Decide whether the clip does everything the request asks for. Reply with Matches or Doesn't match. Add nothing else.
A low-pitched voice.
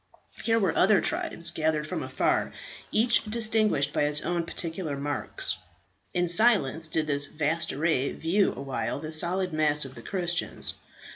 Doesn't match